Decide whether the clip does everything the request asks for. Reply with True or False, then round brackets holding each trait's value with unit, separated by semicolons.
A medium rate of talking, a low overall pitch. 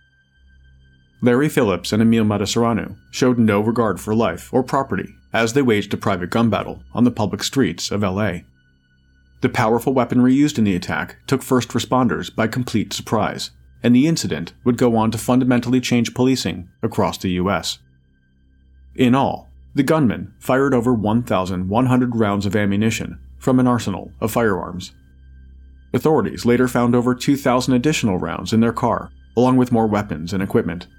True (160 wpm; 110 Hz)